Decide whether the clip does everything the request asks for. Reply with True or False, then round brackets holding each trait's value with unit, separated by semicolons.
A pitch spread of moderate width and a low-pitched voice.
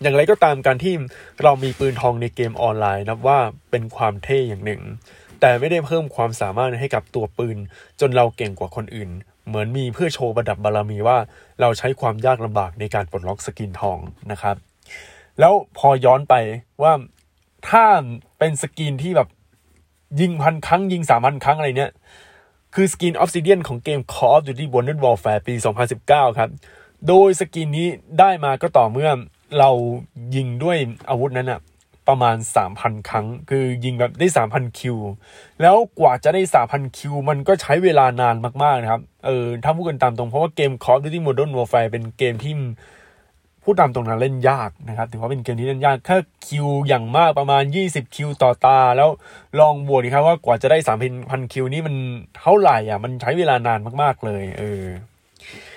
True (4.3 semitones; 125 Hz)